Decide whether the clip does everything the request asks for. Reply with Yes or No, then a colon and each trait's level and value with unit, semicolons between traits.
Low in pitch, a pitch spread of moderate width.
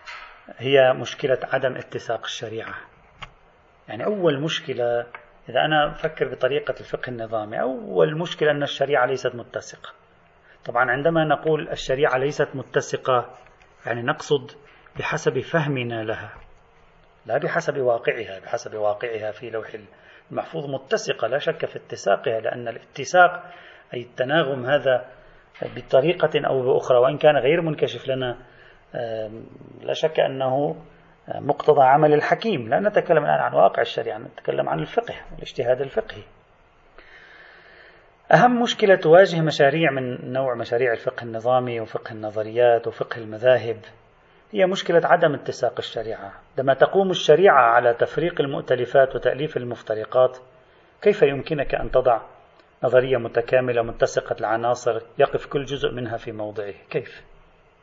Yes: low, 130 Hz; average, 4.3 semitones